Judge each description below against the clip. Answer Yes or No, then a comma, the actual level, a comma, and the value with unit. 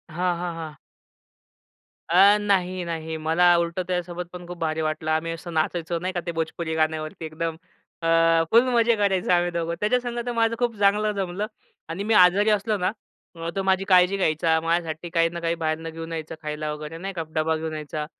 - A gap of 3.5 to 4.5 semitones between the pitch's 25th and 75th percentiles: No, average, 3.1 semitones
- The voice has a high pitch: No, medium, 170 Hz